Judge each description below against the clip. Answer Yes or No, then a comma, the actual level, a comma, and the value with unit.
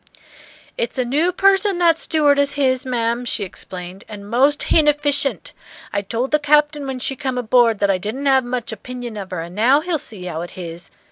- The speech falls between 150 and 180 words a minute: No, average, 195 wpm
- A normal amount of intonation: No, wide, 5.7 semitones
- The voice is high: Yes, very high, 255 Hz